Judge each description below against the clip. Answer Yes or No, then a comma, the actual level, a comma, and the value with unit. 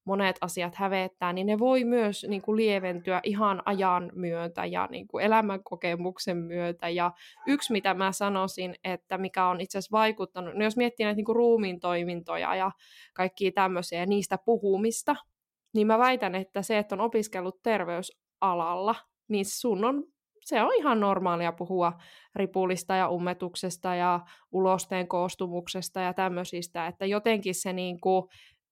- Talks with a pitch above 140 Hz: Yes, high, 190 Hz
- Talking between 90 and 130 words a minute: No, average, 150 wpm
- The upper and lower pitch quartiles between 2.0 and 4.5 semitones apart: Yes, average, 2.8 semitones